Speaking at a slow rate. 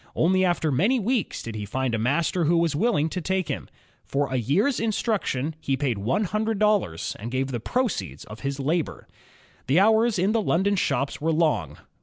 No: average, 195 wpm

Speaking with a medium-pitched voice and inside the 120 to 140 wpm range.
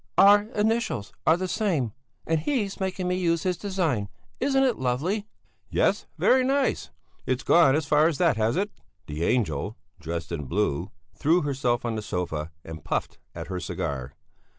No: medium, 155 Hz; average, 170 wpm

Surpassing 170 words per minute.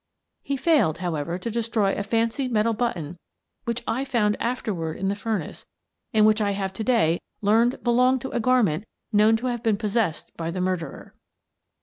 Yes: average, 185 wpm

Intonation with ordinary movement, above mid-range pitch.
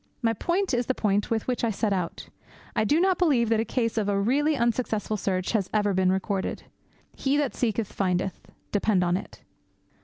Yes: average, 4.1 semitones; high, 220 Hz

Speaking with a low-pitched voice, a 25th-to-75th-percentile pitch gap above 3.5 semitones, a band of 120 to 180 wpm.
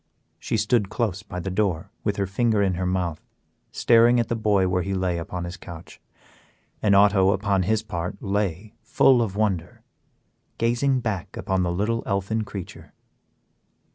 No: low, 100 Hz; average, 3.1 semitones; average, 165 wpm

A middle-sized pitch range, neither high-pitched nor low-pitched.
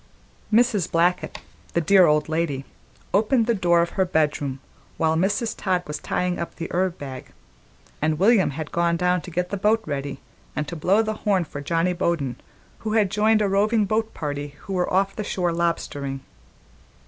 Yes: average, 4.4 semitones; medium, 175 Hz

